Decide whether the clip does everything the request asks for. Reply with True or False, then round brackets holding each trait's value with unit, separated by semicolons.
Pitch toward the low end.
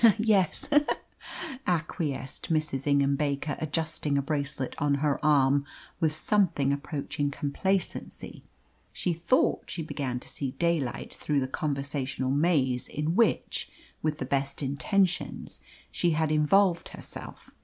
False (150 Hz)